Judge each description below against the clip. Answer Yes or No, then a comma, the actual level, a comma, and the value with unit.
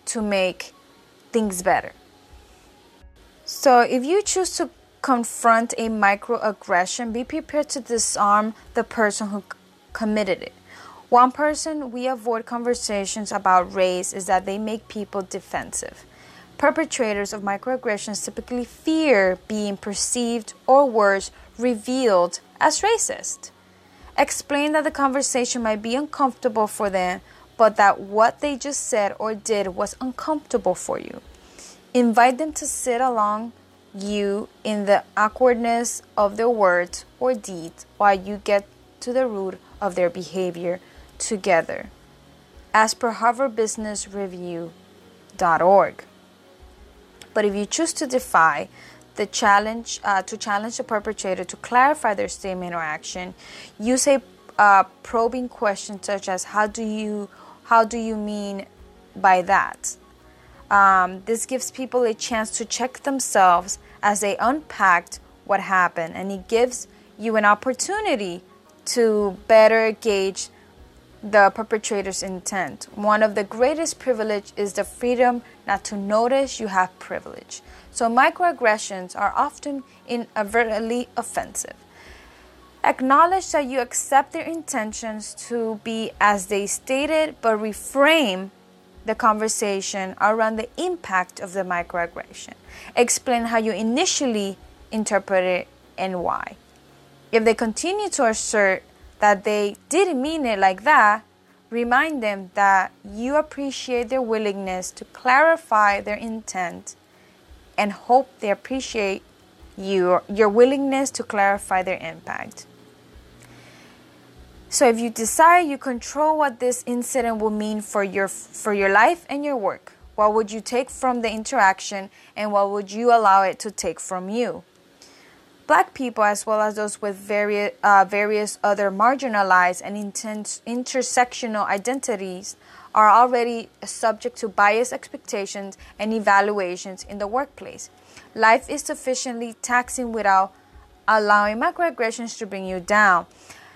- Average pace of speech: No, slow, 130 wpm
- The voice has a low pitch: No, high, 220 Hz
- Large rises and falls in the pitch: No, average, 3.8 semitones